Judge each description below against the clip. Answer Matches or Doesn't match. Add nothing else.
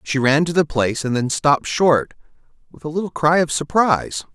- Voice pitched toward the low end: Doesn't match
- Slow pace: Doesn't match